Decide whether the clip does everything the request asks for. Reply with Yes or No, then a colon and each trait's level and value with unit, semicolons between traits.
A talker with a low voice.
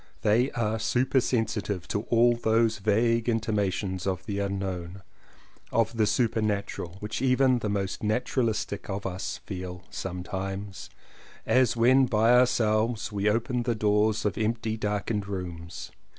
Yes: low, 105 Hz